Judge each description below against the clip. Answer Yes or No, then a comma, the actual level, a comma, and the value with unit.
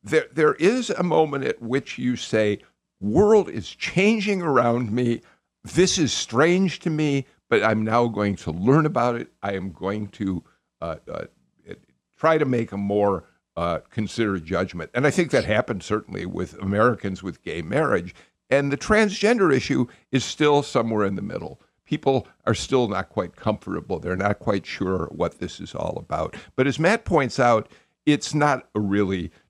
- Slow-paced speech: No, average, 175 wpm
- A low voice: Yes, low, 120 Hz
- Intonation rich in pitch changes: Yes, wide, 7.0 semitones